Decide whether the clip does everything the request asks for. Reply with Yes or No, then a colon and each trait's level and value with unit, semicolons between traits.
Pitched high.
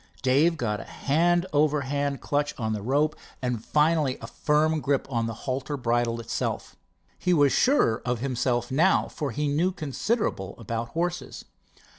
No: medium, 140 Hz